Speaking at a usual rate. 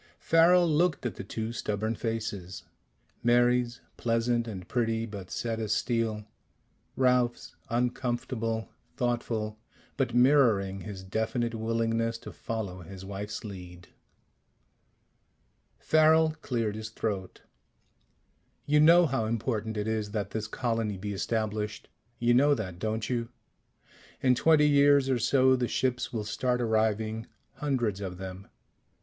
No: slow, 125 wpm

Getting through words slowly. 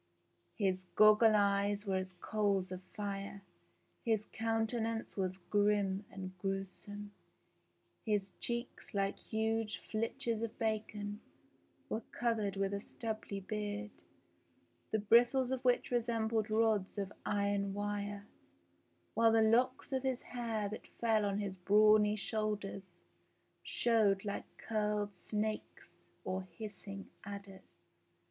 Yes: slow, 115 wpm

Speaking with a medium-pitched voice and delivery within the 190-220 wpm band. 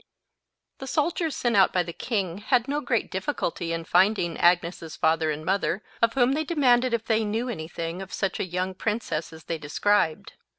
No: high, 195 Hz; average, 195 wpm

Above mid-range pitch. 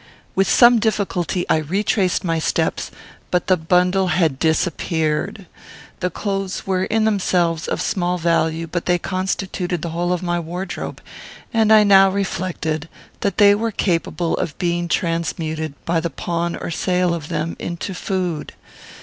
No: medium, 180 Hz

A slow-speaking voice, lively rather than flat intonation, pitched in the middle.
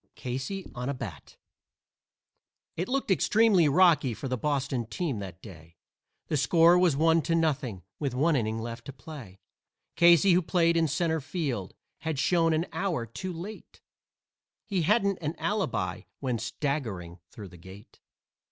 No: average, 150 wpm; wide, 6.6 semitones; medium, 145 Hz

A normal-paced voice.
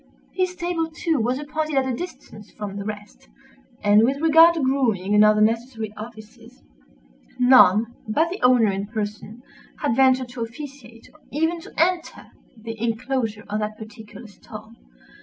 Yes: average, 160 wpm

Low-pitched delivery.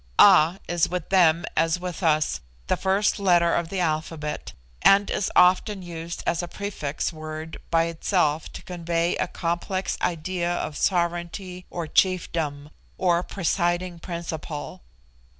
No: medium, 170 Hz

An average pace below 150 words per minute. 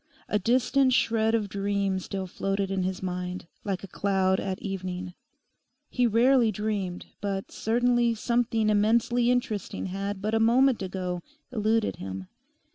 Yes: average, 140 wpm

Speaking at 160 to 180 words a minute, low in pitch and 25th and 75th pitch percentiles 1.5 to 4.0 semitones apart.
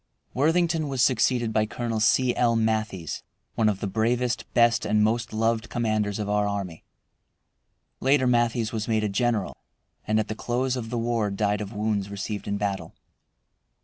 Yes: average, 170 wpm; low, 110 Hz; narrow, 2.5 semitones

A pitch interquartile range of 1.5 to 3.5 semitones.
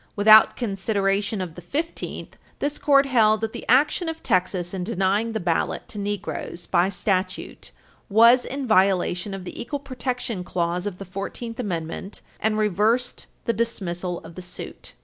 No: average, 4.1 semitones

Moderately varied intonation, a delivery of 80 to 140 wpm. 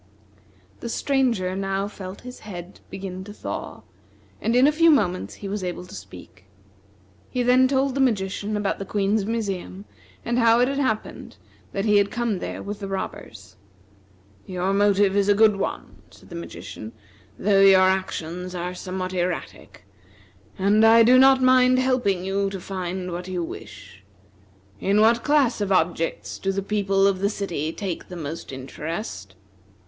No: average, 3.6 semitones; average, 165 wpm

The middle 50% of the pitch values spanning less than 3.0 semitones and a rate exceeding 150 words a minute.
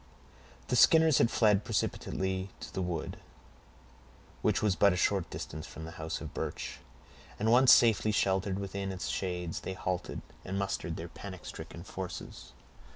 Yes: narrow, 2.4 semitones; average, 160 wpm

